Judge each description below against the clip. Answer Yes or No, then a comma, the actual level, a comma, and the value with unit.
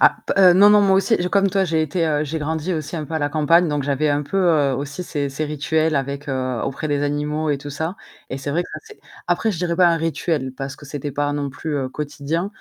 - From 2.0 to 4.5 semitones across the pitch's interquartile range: Yes, average, 2.9 semitones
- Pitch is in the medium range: Yes, medium, 150 Hz